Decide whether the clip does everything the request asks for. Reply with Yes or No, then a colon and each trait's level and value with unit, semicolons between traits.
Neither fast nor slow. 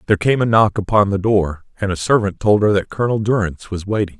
No: fast, 245 wpm